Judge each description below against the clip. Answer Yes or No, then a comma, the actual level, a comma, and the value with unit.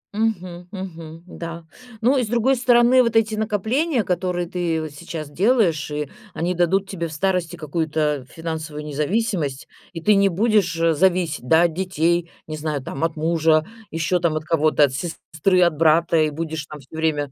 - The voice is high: No, medium, 170 Hz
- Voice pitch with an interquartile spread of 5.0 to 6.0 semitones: No, average, 3.6 semitones